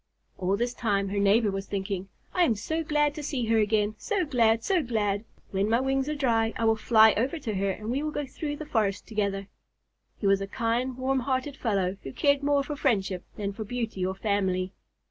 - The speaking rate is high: Yes, fast, 220 wpm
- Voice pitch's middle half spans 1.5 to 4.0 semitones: No, average, 5.1 semitones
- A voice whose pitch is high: Yes, high, 225 Hz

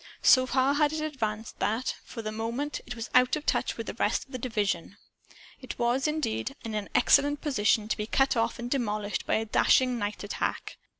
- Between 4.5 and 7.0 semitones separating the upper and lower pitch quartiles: No, average, 4.0 semitones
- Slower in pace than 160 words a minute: No, average, 200 wpm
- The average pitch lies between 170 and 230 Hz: No, high, 240 Hz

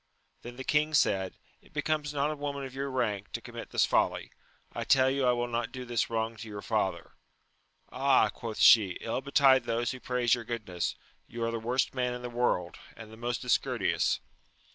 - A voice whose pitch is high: No, low, 120 Hz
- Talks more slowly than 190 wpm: No, fast, 205 wpm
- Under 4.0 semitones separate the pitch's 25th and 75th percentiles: Yes, narrow, 2.5 semitones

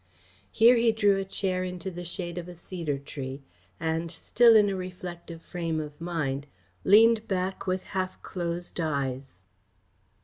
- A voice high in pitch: No, medium, 175 Hz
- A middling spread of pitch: Yes, average, 3.0 semitones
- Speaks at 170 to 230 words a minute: No, average, 150 wpm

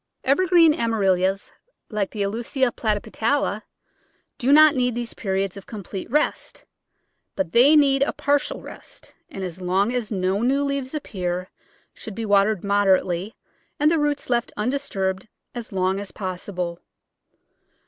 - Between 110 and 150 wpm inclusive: Yes, average, 145 wpm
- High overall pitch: Yes, high, 215 Hz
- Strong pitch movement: Yes, wide, 6.0 semitones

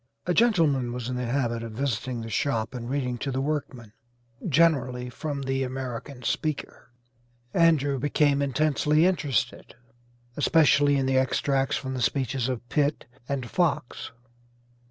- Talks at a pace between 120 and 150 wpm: Yes, average, 140 wpm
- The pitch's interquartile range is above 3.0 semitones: No, average, 2.7 semitones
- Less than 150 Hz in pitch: Yes, low, 135 Hz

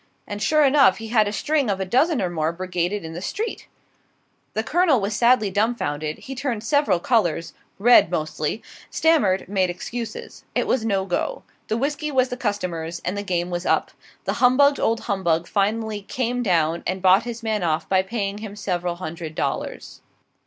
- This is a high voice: Yes, high, 205 Hz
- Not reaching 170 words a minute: No, average, 180 wpm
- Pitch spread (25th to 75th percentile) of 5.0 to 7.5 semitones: Yes, wide, 5.5 semitones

